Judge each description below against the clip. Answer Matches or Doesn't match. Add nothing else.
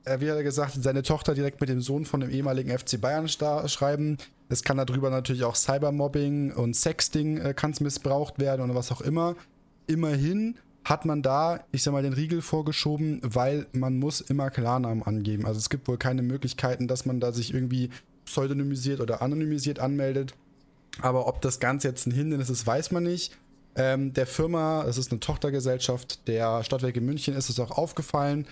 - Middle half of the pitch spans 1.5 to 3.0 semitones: Matches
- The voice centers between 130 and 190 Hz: Matches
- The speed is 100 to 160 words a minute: Doesn't match